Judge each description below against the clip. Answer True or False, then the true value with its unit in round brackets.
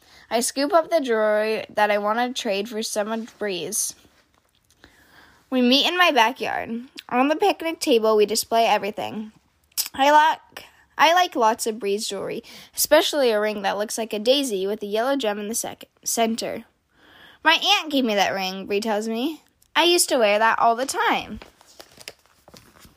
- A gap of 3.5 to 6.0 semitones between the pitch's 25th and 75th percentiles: True (5.0 semitones)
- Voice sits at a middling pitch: False (225 Hz)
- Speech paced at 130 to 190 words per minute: True (175 wpm)